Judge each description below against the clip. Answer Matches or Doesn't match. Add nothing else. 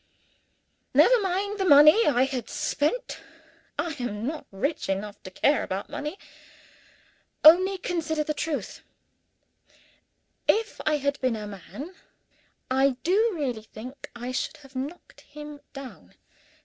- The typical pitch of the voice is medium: Doesn't match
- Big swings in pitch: Doesn't match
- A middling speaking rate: Doesn't match